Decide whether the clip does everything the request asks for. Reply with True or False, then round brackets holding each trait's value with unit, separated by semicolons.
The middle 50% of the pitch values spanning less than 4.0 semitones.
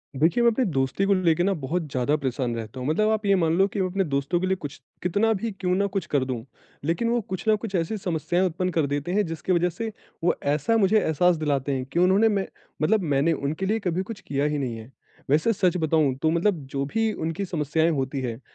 False (5.3 semitones)